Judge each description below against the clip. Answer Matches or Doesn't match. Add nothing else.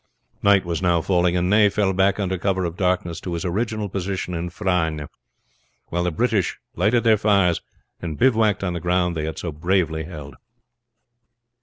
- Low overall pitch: Matches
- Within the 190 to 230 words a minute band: Doesn't match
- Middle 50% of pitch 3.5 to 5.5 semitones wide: Doesn't match